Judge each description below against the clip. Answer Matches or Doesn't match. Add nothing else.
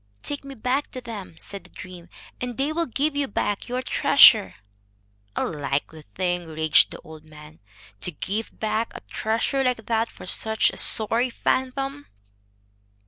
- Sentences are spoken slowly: Doesn't match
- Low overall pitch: Doesn't match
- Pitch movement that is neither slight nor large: Doesn't match